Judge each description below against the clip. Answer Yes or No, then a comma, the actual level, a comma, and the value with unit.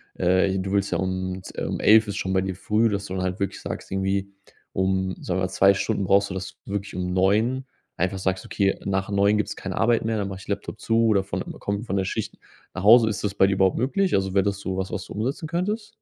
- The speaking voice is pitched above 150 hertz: No, low, 100 Hz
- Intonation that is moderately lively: No, narrow, 1.9 semitones